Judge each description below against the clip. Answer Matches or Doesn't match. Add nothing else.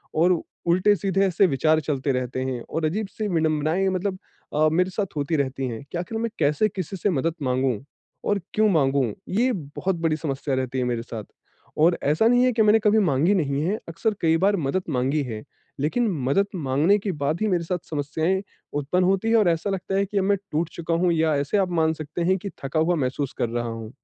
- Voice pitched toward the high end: Doesn't match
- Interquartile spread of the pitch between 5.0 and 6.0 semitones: Matches